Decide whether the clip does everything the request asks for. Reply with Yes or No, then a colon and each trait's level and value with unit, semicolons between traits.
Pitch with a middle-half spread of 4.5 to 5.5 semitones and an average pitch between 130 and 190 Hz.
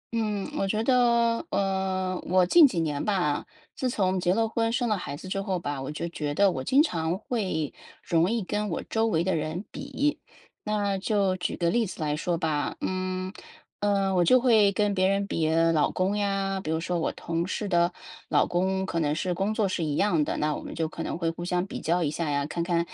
No: average, 3.7 semitones; medium, 185 Hz